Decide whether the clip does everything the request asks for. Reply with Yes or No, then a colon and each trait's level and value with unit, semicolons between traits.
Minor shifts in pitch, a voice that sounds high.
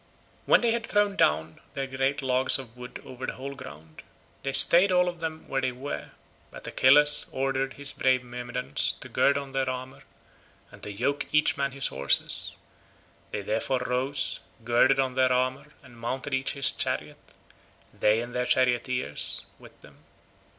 No: narrow, 2.0 semitones; low, 130 Hz